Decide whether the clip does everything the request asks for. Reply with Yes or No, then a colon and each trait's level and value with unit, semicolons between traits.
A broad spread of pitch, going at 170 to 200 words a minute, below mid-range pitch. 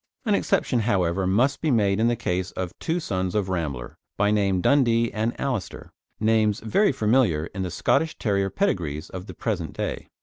No: average, 4.3 semitones; average, 180 wpm; low, 105 Hz